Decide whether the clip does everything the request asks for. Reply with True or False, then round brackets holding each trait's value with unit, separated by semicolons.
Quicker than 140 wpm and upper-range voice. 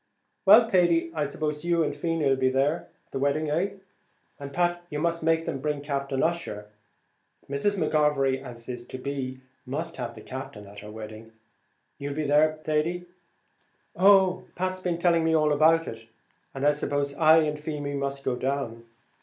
False (170 wpm; 150 Hz)